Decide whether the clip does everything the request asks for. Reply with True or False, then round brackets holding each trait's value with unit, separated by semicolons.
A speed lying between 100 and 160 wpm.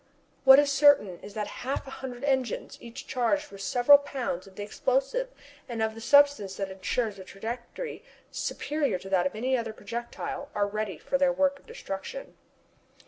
False (180 wpm)